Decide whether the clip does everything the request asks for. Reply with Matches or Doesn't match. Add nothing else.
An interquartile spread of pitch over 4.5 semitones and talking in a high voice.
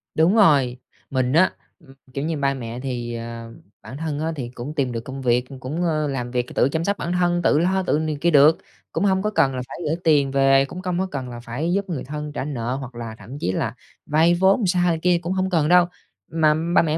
Doesn't match